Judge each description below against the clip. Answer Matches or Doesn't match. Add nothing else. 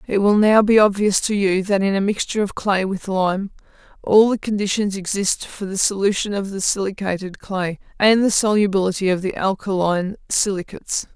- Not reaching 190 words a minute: Matches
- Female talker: Matches